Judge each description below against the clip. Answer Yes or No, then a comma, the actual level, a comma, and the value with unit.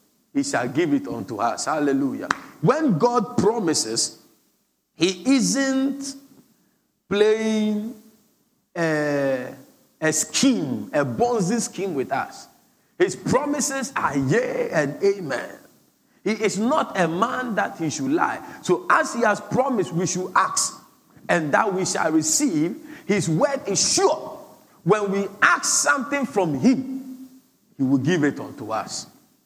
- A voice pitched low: No, high, 230 Hz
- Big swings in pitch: Yes, wide, 6.4 semitones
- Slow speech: Yes, slow, 130 wpm